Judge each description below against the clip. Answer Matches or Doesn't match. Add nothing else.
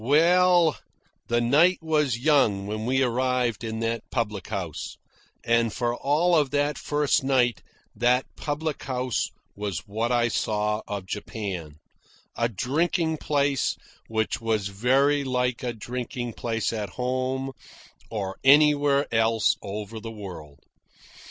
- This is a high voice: Doesn't match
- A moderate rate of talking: Doesn't match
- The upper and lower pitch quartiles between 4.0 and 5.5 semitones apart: Matches